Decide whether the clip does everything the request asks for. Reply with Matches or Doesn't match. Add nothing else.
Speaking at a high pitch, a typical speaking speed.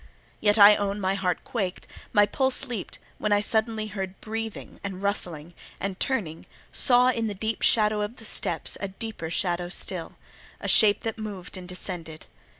Matches